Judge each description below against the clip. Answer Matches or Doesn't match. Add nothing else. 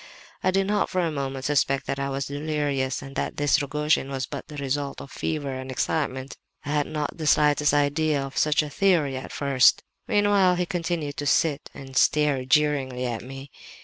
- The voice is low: Doesn't match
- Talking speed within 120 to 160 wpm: Doesn't match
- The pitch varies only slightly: Matches